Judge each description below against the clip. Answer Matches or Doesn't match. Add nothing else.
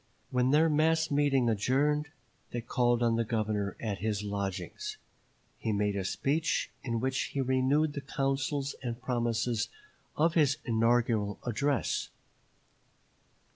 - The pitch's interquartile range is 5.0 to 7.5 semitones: Doesn't match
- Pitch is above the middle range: Doesn't match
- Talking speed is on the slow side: Matches